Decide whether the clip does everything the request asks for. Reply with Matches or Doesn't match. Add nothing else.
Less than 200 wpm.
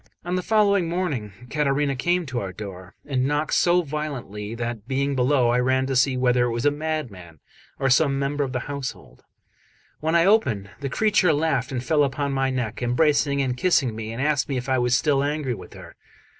Doesn't match